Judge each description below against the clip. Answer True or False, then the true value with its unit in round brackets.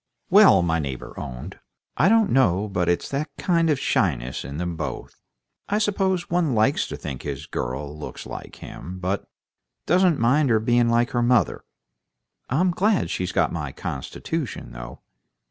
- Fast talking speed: False (165 wpm)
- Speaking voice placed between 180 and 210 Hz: False (120 Hz)